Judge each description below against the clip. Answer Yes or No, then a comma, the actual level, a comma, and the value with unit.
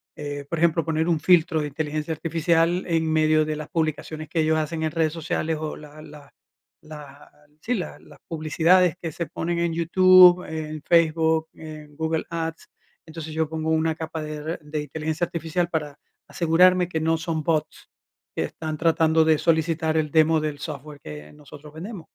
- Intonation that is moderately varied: No, narrow, 1.4 semitones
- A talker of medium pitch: Yes, medium, 160 Hz